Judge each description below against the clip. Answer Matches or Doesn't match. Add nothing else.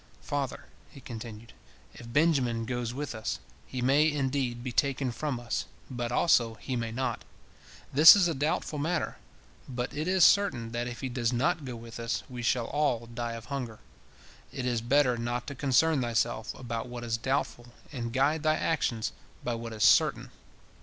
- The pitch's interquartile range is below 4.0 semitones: Matches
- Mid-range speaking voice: Doesn't match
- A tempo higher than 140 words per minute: Matches